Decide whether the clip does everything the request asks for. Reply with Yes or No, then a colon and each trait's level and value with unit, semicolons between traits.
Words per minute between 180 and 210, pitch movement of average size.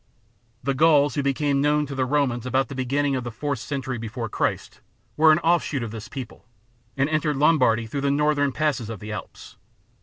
Yes: average, 195 wpm; average, 3.2 semitones